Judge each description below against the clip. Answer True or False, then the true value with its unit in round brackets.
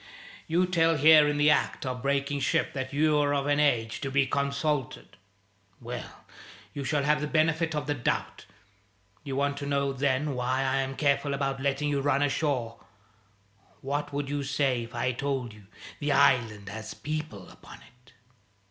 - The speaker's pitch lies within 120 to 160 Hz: True (140 Hz)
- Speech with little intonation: True (1.9 semitones)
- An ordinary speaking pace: True (170 wpm)